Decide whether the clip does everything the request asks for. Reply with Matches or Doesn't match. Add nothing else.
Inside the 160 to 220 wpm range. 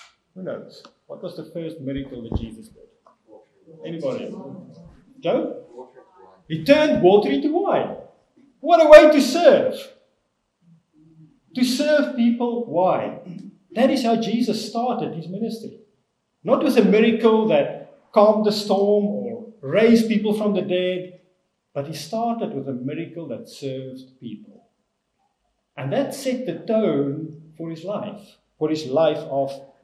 Doesn't match